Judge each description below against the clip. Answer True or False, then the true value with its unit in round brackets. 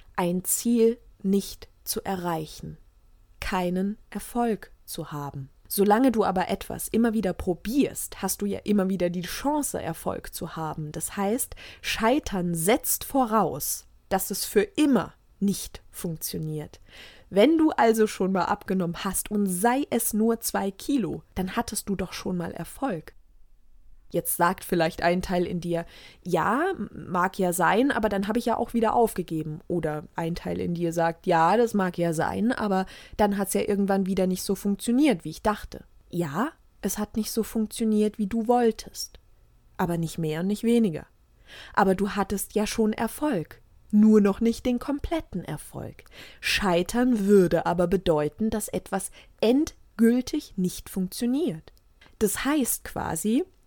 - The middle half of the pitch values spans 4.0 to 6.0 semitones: True (4.6 semitones)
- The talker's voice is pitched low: False (200 Hz)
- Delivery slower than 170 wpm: True (155 wpm)